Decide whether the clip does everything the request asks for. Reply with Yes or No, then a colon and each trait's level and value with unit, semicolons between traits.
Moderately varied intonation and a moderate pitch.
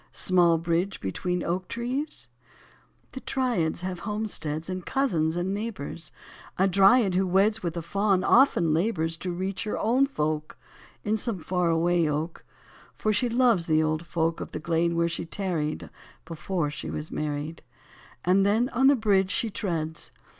Yes: average, 4.3 semitones; medium, 180 Hz